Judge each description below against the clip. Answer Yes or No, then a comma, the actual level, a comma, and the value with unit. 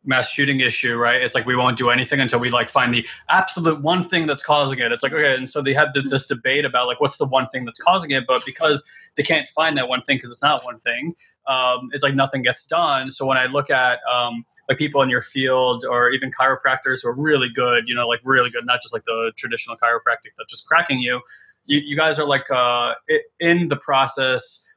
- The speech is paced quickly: Yes, fast, 245 wpm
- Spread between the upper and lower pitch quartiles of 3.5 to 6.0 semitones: No, average, 3.0 semitones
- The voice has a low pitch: Yes, low, 130 Hz